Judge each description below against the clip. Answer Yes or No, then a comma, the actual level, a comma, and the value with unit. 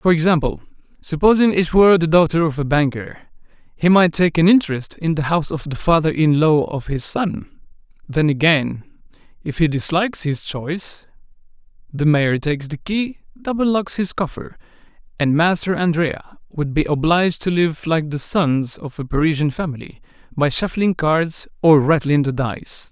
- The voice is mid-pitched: Yes, medium, 160 Hz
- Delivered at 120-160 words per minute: No, average, 170 wpm